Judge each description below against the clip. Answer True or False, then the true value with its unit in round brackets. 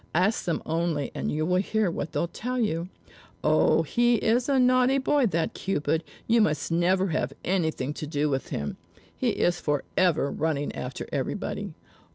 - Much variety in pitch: True (6.3 semitones)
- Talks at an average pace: True (170 wpm)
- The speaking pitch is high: False (175 Hz)